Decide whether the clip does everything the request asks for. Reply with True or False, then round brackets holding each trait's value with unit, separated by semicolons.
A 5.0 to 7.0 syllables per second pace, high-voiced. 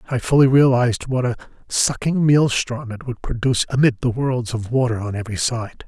False (5.3 syllables/s; 125 Hz)